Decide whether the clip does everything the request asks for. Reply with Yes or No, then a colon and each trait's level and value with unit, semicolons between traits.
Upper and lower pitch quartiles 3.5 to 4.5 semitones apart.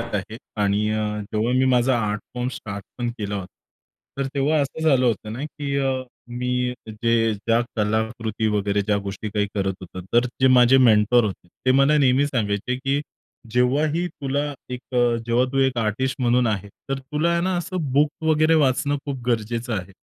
Yes: average, 4.0 semitones